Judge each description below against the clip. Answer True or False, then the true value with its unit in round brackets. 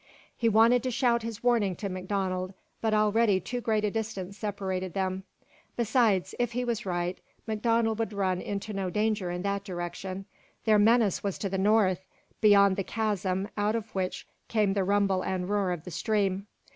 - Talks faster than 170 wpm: True (180 wpm)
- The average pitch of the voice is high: True (200 Hz)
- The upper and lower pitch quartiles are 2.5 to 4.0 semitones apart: True (2.8 semitones)